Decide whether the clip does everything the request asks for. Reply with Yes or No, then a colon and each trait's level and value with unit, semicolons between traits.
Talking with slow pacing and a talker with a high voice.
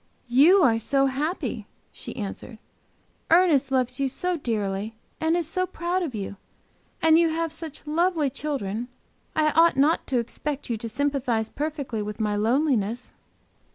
No: average, 155 wpm; very high, 275 Hz